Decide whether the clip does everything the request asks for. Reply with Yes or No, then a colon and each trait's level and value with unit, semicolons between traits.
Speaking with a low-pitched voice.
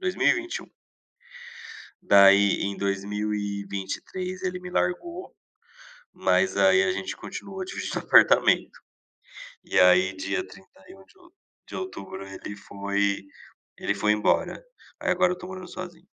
Yes: low, 105 Hz